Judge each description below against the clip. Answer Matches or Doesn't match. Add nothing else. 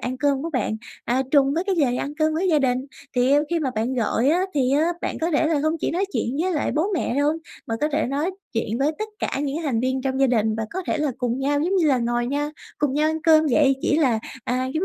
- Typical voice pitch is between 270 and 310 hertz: Matches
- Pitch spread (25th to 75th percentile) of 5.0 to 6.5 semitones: Doesn't match